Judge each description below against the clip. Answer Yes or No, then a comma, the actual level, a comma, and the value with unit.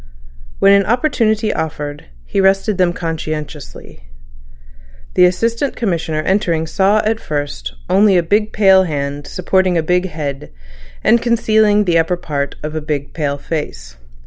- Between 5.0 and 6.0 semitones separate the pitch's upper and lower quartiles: Yes, average, 5.3 semitones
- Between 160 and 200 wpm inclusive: No, average, 145 wpm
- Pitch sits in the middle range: Yes, medium, 175 Hz